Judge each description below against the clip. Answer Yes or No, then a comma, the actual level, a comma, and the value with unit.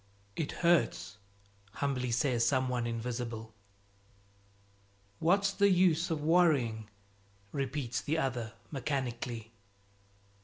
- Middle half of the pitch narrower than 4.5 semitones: No, average, 5.2 semitones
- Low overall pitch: Yes, low, 130 Hz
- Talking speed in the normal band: No, slow, 90 wpm